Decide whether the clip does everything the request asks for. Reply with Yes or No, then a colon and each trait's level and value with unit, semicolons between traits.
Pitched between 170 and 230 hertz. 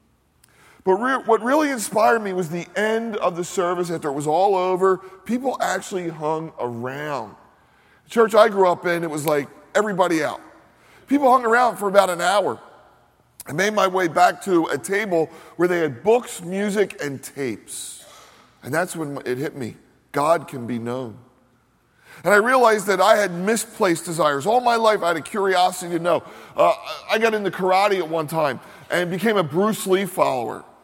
Yes: medium, 185 Hz